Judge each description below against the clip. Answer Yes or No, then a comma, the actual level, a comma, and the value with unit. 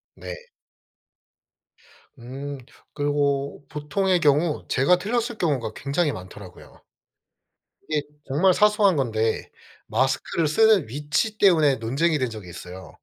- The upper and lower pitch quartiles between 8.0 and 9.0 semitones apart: No, wide, 5.6 semitones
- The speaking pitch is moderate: Yes, medium, 145 Hz